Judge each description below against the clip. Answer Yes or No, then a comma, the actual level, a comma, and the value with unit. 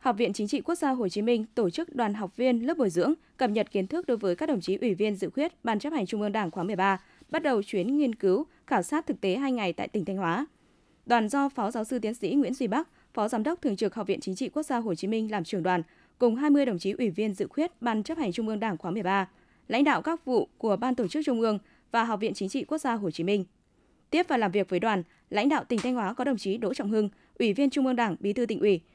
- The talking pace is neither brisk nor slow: No, fast, 295 wpm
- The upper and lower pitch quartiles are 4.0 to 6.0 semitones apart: Yes, average, 5.3 semitones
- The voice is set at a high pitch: Yes, high, 230 Hz